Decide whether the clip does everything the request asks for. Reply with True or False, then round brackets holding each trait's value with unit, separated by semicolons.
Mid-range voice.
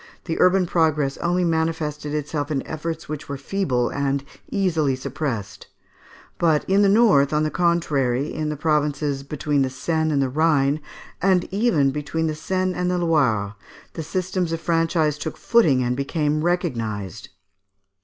True (155 Hz)